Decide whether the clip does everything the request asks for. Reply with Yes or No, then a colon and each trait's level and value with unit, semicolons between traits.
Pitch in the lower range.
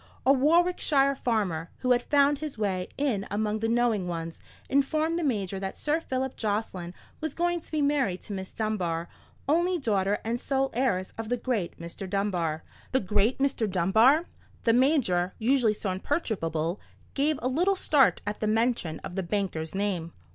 No: high, 220 Hz